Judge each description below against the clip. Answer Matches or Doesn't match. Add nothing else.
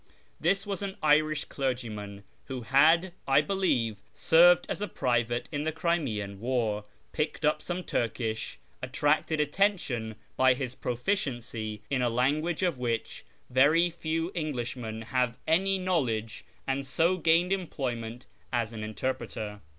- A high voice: Doesn't match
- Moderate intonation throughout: Doesn't match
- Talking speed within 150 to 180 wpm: Doesn't match